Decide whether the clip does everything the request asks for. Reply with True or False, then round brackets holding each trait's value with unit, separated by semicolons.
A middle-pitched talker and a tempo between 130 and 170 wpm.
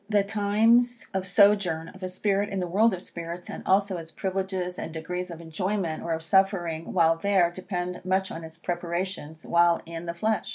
False (180 Hz; 195 wpm)